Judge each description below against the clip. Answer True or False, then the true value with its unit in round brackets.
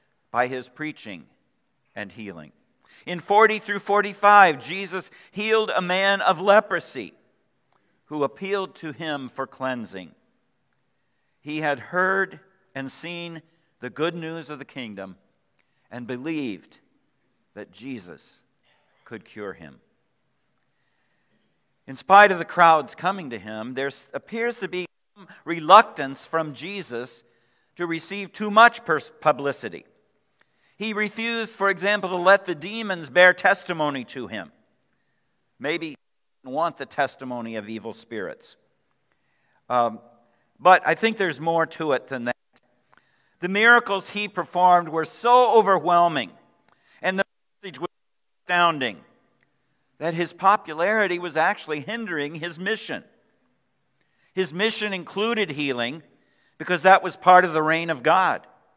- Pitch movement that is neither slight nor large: False (6.0 semitones)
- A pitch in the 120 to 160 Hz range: False (170 Hz)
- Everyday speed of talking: False (130 wpm)